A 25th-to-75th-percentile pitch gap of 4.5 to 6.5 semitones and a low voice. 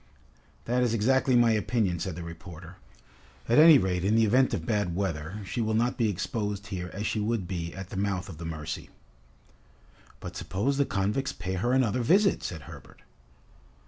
Yes: average, 4.9 semitones; low, 100 Hz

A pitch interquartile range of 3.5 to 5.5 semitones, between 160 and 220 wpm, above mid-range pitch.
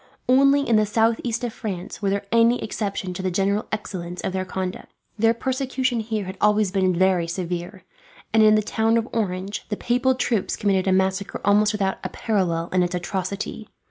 No: average, 3.1 semitones; average, 190 wpm; high, 205 Hz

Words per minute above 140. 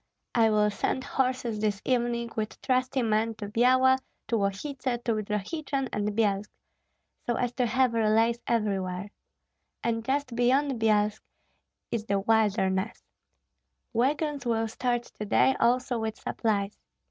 No: slow, 135 wpm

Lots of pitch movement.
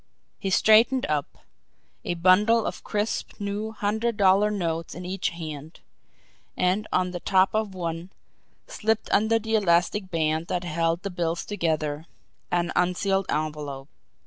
No: average, 3.9 semitones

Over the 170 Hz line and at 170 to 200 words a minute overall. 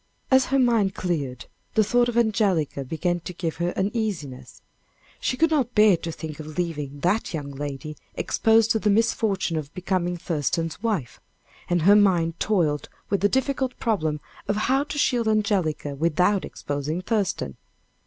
No: medium, 185 Hz; average, 160 wpm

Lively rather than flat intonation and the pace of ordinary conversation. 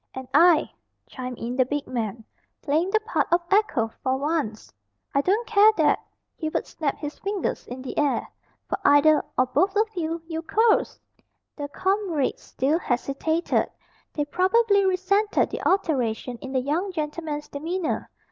Yes: wide, 5.7 semitones; average, 155 wpm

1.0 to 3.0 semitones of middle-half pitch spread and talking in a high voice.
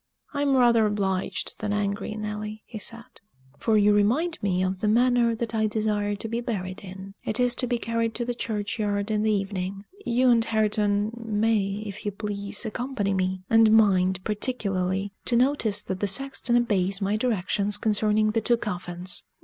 Yes: narrow, 2.5 semitones; high, 210 Hz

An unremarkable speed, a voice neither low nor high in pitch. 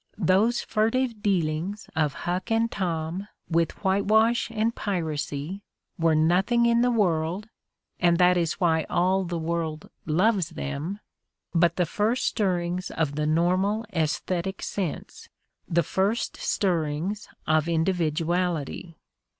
No: slow, 130 wpm; medium, 180 Hz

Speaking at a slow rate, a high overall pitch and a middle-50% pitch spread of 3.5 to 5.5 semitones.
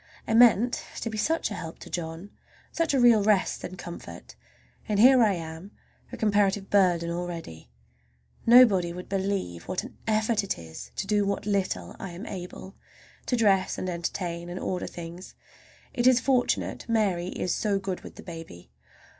No: average, 170 wpm; high, 195 Hz; average, 3.9 semitones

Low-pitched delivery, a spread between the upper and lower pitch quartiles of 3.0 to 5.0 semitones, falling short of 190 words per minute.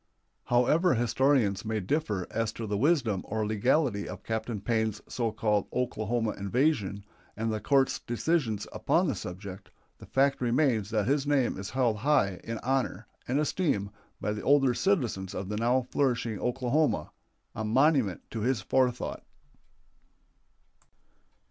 Yes: low, 115 Hz; average, 4.3 semitones; average, 140 wpm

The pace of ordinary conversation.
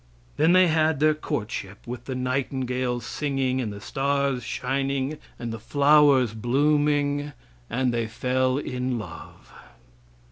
No: slow, 130 wpm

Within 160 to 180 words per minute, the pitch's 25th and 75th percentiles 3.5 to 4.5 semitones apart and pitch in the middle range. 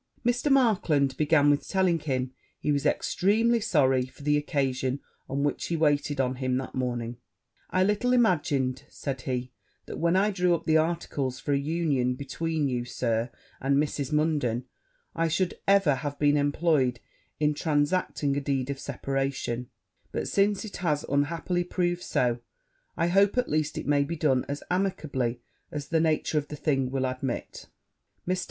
Yes: average, 170 wpm; average, 4.2 semitones; medium, 145 Hz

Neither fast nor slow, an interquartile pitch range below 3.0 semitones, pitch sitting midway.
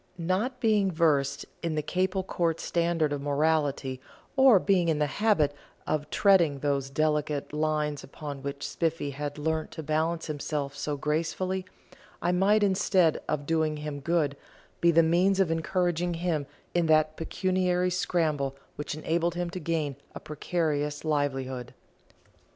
No: average, 145 wpm; average, 3.3 semitones; medium, 160 Hz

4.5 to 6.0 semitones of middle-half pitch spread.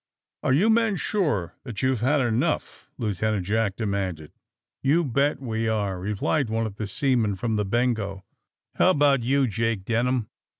Yes: average, 4.8 semitones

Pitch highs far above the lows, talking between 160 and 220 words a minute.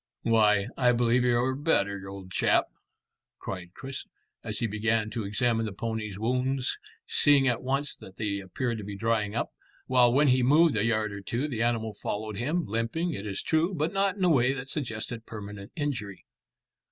No: average, 3.9 semitones; average, 185 wpm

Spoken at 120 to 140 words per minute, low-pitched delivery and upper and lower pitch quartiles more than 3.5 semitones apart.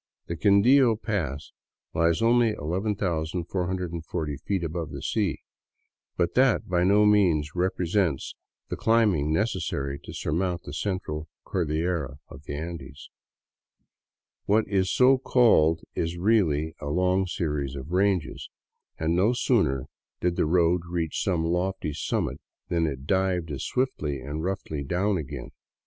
Yes: slow, 135 wpm; very low, 85 Hz; average, 4.2 semitones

